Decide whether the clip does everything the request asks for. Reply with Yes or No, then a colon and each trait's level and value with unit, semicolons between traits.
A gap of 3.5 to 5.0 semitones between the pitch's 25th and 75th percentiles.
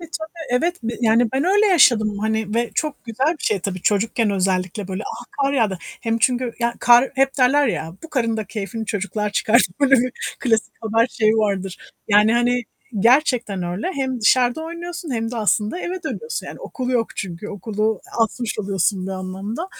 Yes: average, 3.9 semitones